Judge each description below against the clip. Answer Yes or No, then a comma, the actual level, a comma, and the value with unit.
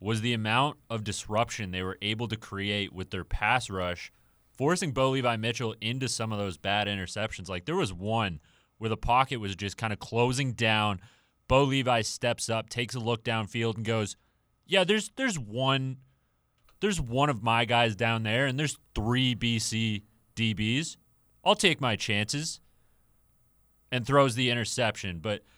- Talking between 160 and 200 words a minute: Yes, average, 170 wpm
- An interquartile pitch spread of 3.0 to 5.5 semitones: Yes, average, 3.4 semitones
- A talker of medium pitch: No, low, 115 Hz